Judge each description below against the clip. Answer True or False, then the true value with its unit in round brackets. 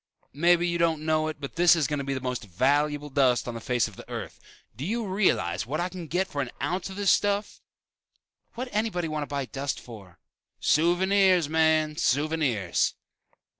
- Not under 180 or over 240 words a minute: True (195 wpm)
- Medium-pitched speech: True (155 Hz)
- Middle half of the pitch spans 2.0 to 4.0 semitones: False (4.4 semitones)